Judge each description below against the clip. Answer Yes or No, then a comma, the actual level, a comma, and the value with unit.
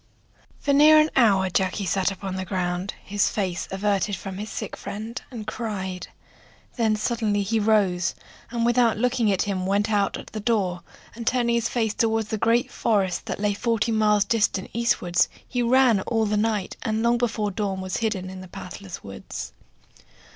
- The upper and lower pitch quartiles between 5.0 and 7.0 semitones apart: No, average, 3.3 semitones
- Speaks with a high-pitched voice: Yes, high, 210 Hz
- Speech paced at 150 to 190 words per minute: Yes, average, 180 wpm